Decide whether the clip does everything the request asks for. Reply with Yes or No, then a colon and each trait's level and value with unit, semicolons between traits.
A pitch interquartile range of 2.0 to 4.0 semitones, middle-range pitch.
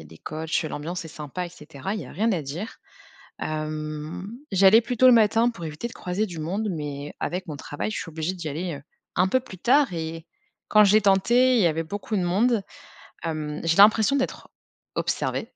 No: wide, 5.5 semitones; medium, 180 Hz